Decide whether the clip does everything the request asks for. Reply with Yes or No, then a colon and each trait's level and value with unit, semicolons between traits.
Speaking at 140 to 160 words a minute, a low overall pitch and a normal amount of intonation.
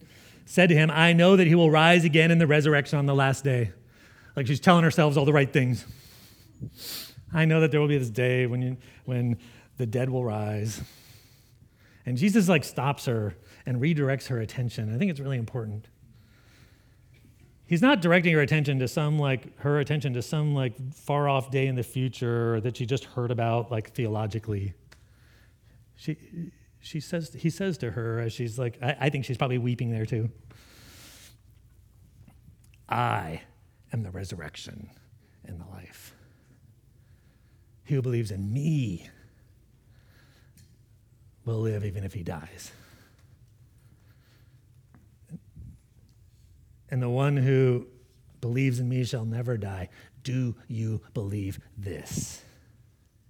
Yes: average, 145 wpm; low, 120 Hz; average, 3.3 semitones